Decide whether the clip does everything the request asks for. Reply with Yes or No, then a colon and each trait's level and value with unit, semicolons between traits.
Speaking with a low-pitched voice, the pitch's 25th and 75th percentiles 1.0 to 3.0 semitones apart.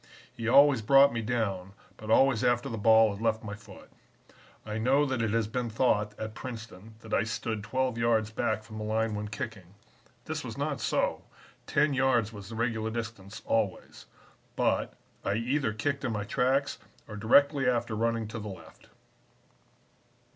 Yes: low, 115 Hz; narrow, 2.4 semitones